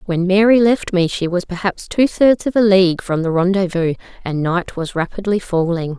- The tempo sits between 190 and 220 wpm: Yes, average, 200 wpm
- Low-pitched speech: No, medium, 185 Hz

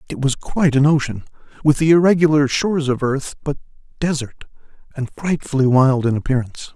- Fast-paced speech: No, average, 160 wpm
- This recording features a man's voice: Yes, male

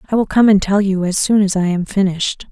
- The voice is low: No, high, 195 Hz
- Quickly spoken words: Yes, fast, 285 wpm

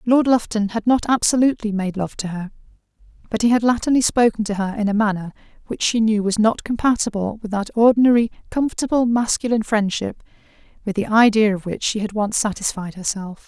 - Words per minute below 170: No, average, 185 wpm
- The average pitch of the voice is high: Yes, high, 215 Hz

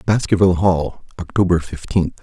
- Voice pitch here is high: No, very low, 90 Hz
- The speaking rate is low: Yes, slow, 110 wpm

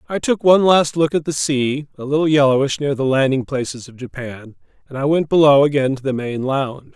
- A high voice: No, medium, 140 Hz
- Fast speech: Yes, fast, 225 wpm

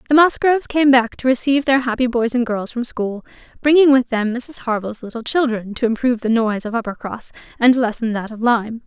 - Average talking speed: No, fast, 210 wpm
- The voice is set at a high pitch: Yes, high, 240 Hz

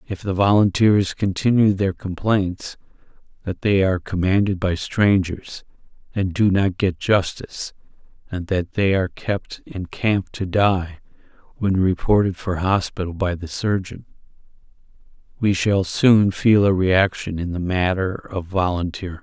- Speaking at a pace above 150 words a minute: No, slow, 135 wpm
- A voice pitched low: Yes, very low, 95 Hz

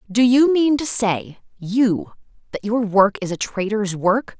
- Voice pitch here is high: Yes, high, 220 Hz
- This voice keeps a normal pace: Yes, average, 175 wpm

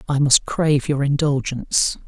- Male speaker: Yes, male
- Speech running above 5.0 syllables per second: No, 4.9 syllables/s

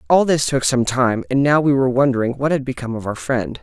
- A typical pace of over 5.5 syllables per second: Yes, 6.2 syllables/s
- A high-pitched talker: No, low, 130 Hz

